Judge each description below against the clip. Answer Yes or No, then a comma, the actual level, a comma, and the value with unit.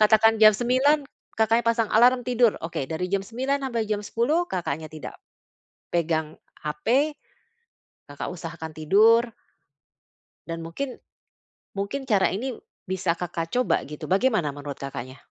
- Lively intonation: Yes, wide, 6.4 semitones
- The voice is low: No, high, 200 Hz